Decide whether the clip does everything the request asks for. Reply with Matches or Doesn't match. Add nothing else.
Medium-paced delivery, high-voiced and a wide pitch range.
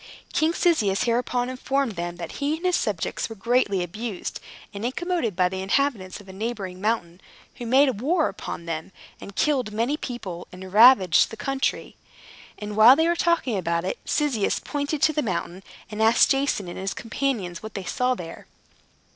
Matches